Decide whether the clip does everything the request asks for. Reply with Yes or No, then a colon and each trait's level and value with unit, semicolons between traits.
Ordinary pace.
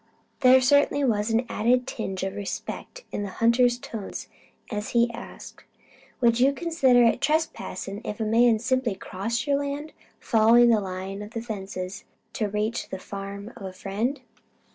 Yes: average, 165 wpm